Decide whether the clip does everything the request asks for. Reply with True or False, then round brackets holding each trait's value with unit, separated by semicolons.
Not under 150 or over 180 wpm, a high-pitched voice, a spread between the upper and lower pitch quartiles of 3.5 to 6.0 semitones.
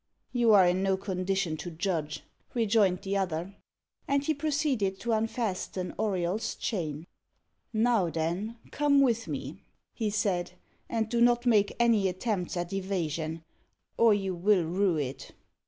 False (140 wpm; 195 Hz; 4.3 semitones)